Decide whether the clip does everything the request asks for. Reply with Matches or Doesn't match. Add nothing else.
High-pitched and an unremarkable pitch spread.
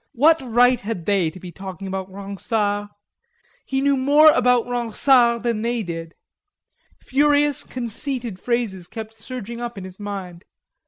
Matches